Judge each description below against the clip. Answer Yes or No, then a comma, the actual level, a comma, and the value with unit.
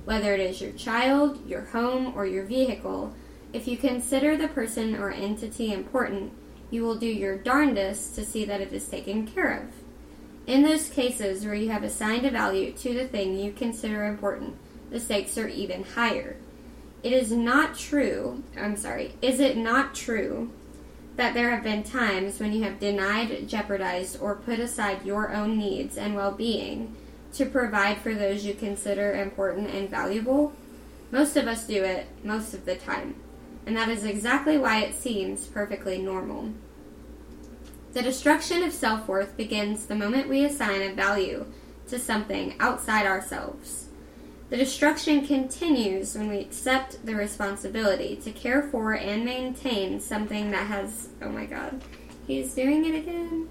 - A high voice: Yes, high, 220 Hz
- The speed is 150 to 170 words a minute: Yes, average, 165 wpm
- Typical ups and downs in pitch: Yes, average, 4.4 semitones